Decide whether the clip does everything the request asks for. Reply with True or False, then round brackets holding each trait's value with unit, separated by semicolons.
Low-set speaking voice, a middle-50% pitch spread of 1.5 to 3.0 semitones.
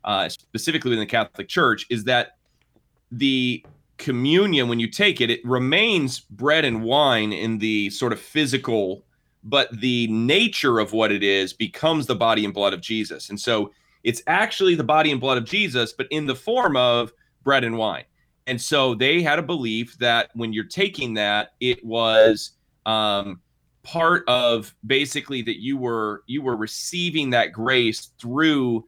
False (120 Hz; 3.8 semitones)